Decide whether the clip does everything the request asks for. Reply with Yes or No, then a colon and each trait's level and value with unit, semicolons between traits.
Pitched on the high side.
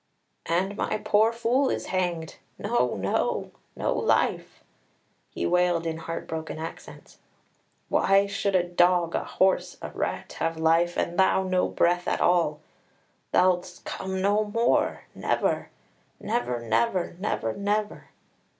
No: medium, 180 Hz